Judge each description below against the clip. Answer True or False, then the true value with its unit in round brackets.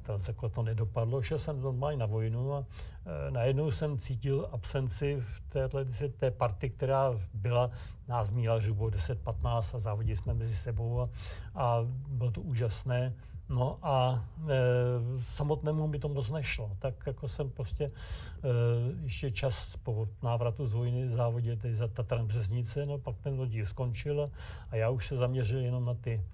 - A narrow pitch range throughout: False (3.2 semitones)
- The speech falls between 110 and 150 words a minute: False (170 wpm)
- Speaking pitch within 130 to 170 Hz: False (120 Hz)